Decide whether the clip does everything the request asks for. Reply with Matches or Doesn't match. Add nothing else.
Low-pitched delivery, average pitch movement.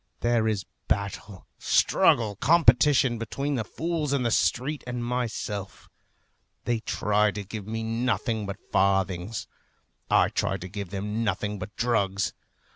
Matches